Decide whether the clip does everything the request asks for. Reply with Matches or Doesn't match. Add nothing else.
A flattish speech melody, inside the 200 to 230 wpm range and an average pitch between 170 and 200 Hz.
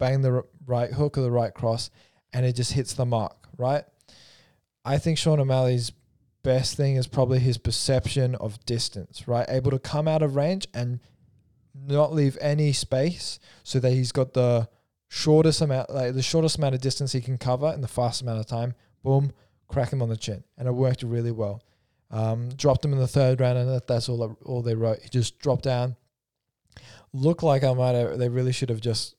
Doesn't match